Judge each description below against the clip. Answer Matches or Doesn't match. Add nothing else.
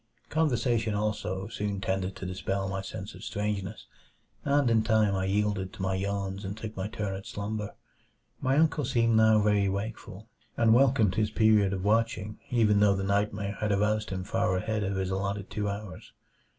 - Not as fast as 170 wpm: Doesn't match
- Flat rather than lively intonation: Matches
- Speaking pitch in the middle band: Doesn't match